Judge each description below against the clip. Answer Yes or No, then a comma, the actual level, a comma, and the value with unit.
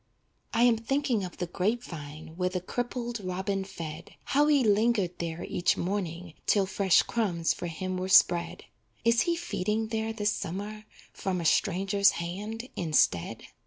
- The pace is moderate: Yes, average, 160 wpm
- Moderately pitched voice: No, high, 195 Hz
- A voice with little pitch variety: No, average, 4.3 semitones